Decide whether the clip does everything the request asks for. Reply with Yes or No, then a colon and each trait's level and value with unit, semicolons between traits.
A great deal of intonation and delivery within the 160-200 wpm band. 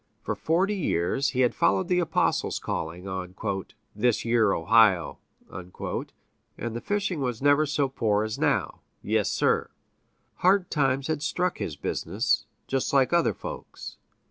No: wide, 7.2 semitones; average, 145 wpm